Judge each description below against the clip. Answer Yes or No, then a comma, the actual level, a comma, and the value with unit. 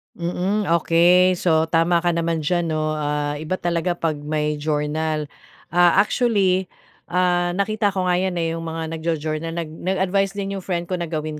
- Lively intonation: No, narrow, 2.6 semitones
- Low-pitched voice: No, medium, 170 Hz